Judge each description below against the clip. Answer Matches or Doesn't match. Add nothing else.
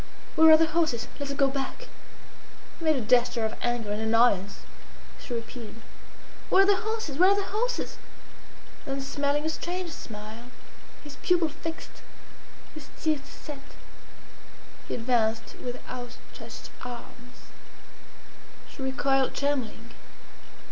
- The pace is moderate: Doesn't match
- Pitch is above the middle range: Matches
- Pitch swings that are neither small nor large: Matches